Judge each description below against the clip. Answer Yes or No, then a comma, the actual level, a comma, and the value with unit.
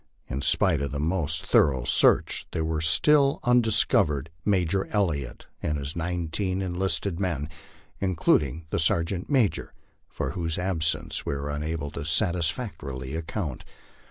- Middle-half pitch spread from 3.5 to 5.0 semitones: Yes, average, 4.2 semitones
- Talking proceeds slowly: Yes, slow, 130 wpm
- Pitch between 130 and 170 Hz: No, very low, 85 Hz